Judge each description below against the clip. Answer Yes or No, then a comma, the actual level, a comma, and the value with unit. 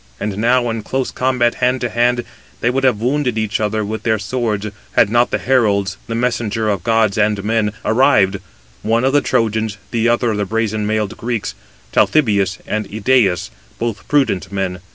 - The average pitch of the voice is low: Yes, low, 110 Hz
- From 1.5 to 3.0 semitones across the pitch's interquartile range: Yes, average, 2.7 semitones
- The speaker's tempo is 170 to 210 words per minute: Yes, average, 180 wpm